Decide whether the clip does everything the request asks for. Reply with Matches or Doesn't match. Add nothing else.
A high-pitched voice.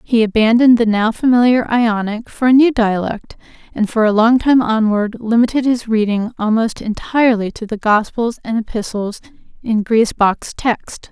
Matches